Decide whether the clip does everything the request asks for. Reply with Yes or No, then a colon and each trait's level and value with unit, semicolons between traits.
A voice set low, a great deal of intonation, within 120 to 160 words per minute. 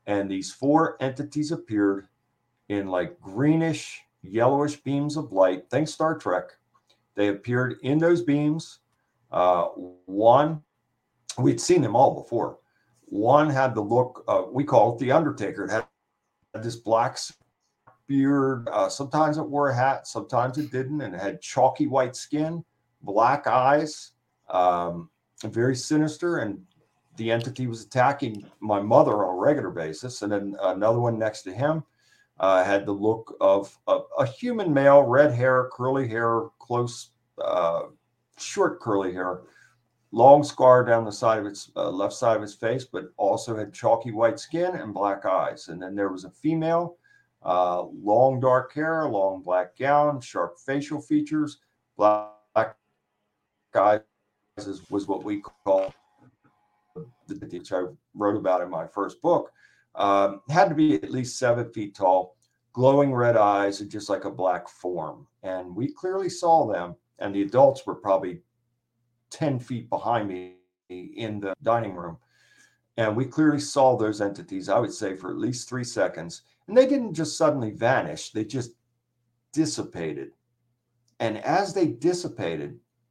Yes: low, 120 Hz; wide, 6.0 semitones; average, 155 wpm